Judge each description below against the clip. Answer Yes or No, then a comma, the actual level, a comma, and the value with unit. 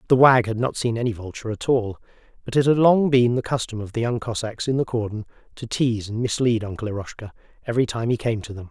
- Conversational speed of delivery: No, fast, 240 wpm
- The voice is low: Yes, low, 115 Hz